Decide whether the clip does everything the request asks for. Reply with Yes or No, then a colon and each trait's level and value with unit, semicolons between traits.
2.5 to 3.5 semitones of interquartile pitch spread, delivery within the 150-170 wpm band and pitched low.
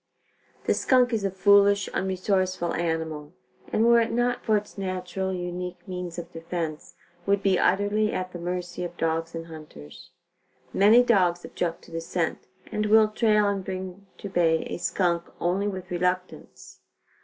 No: average, 2.8 semitones; average, 160 wpm; medium, 185 Hz